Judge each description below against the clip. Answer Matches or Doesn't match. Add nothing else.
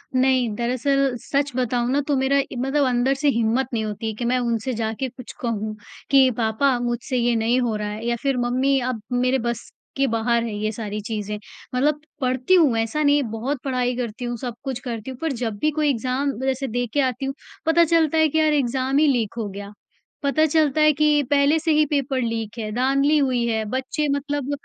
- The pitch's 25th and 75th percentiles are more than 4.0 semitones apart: Doesn't match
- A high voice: Matches